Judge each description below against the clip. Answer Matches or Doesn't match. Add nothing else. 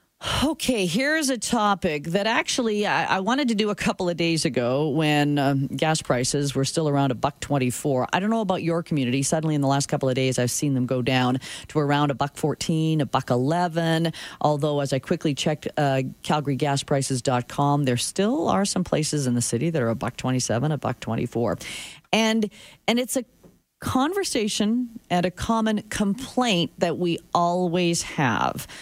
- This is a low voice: Doesn't match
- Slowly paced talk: Doesn't match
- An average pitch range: Doesn't match